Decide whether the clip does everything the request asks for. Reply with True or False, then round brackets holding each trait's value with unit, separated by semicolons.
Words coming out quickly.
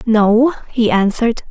False (120 wpm)